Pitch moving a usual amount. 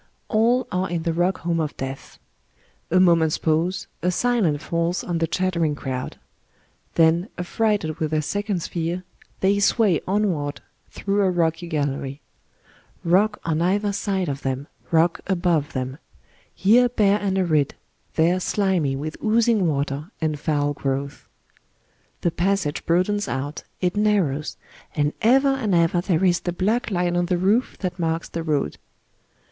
Yes: average, 4.1 semitones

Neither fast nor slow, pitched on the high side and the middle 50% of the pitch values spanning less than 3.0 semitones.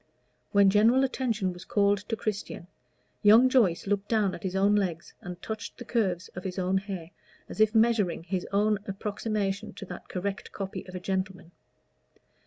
Yes: average, 175 wpm; high, 200 Hz; narrow, 2.5 semitones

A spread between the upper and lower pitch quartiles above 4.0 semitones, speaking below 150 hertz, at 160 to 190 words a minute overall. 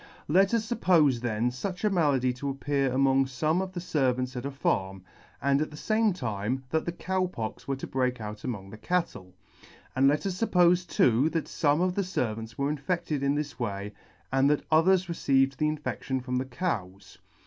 No: wide, 5.5 semitones; medium, 140 Hz; fast, 205 wpm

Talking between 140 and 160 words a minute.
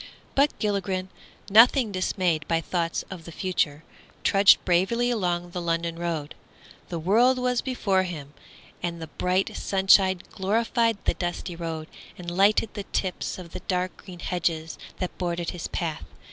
Yes: average, 150 wpm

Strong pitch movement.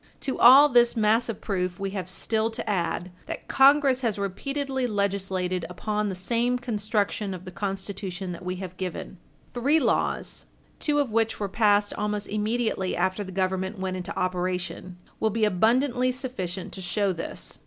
No: average, 4.0 semitones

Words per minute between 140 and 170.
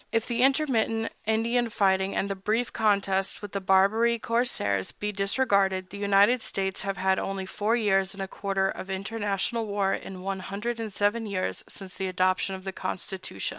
No: average, 185 wpm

